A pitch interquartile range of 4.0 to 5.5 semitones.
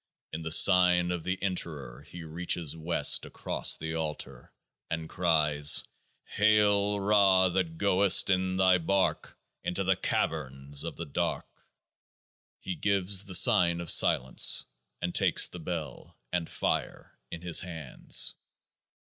No: average, 2.7 semitones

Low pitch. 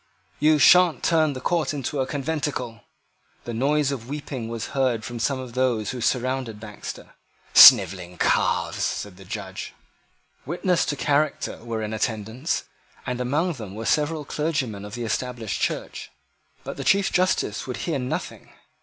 Yes: low, 130 Hz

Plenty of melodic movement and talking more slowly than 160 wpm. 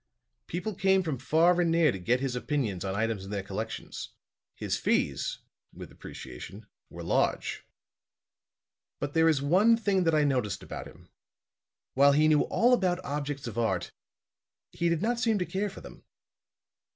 No: wide, 7.3 semitones; average, 165 wpm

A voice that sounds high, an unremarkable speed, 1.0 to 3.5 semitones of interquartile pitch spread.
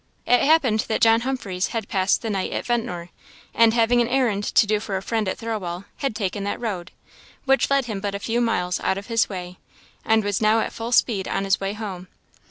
No: high, 215 Hz; fast, 225 wpm; average, 3.1 semitones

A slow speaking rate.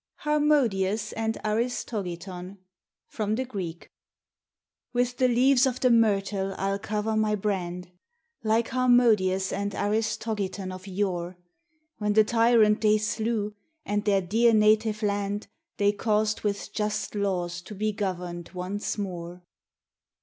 Yes: slow, 125 wpm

